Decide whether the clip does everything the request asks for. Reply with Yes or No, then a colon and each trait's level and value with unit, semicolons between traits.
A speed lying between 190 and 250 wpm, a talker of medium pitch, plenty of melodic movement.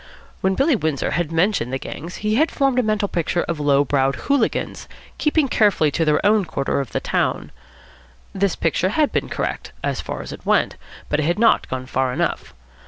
Yes: average, 200 wpm; medium, 175 Hz; wide, 6.7 semitones